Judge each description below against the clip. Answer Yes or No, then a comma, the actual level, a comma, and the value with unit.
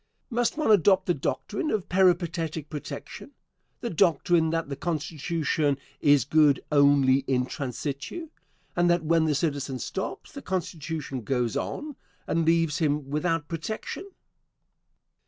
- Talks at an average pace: No, slow, 130 wpm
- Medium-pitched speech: Yes, medium, 160 Hz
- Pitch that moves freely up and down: No, average, 3.6 semitones